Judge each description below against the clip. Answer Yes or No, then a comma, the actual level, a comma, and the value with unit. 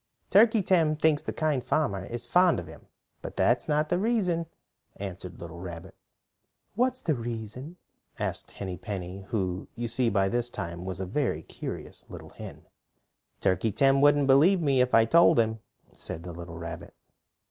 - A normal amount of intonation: No, wide, 8.5 semitones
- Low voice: Yes, low, 120 Hz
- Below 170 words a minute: No, average, 175 wpm